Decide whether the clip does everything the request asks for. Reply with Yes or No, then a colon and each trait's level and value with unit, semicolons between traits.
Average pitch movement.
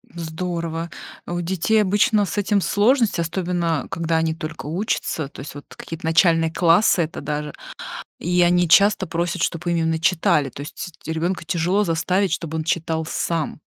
No: narrow, 2.2 semitones